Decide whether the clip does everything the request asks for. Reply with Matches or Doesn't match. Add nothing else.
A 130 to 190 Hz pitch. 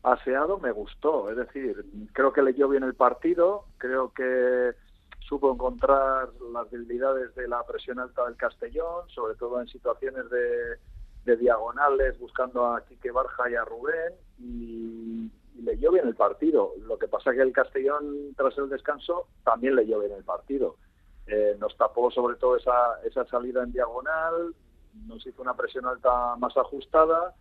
Matches